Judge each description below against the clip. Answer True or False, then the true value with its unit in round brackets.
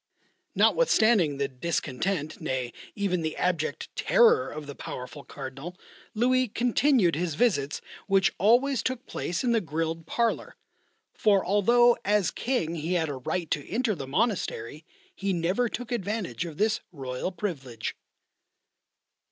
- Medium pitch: True (180 Hz)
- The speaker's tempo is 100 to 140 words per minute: True (135 wpm)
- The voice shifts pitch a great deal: True (7.0 semitones)